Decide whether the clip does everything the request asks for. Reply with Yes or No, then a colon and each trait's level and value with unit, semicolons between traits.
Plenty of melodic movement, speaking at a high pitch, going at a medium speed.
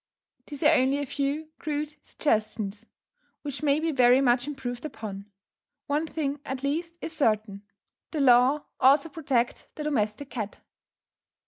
No: average, 3.8 semitones; very high, 275 Hz; average, 145 wpm